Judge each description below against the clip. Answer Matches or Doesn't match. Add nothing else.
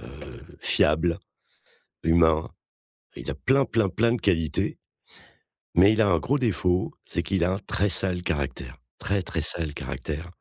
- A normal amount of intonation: Matches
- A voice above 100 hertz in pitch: Doesn't match